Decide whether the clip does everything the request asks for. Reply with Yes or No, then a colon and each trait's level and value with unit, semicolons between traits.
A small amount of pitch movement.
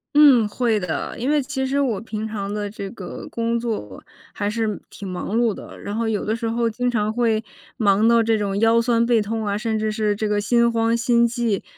Yes: narrow, 2.1 semitones